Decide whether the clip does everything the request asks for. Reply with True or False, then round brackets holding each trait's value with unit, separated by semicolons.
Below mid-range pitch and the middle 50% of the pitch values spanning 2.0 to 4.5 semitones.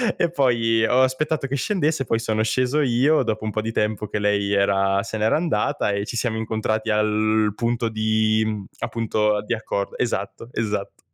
True (110 Hz; 2.5 semitones)